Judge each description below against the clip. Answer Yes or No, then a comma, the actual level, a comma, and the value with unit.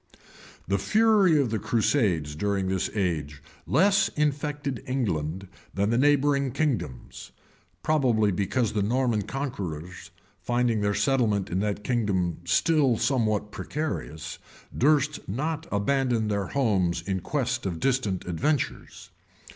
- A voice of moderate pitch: No, low, 115 Hz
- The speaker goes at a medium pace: No, slow, 120 wpm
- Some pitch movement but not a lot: No, wide, 6.3 semitones